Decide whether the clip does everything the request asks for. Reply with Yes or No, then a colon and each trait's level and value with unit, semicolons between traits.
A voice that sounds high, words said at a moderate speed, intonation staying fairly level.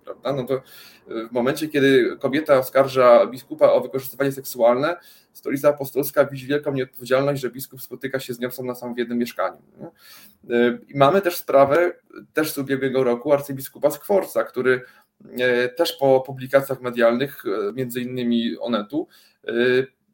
No: low, 135 Hz; average, 125 wpm; narrow, 2.1 semitones